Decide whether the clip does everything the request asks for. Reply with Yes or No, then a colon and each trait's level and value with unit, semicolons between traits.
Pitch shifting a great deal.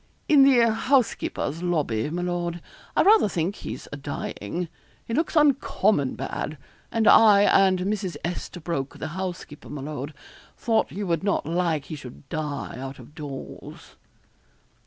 Yes: wide, 5.8 semitones